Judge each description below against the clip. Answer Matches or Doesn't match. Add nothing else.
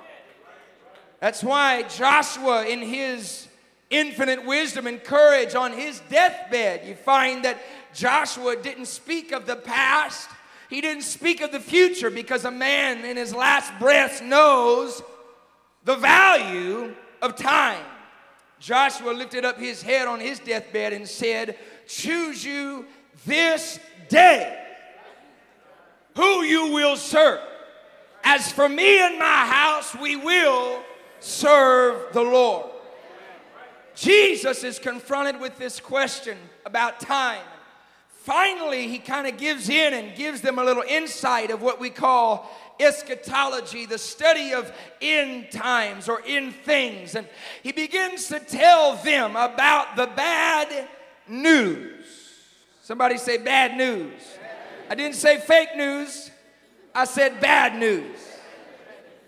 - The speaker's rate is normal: Doesn't match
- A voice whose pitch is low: Doesn't match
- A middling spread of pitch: Matches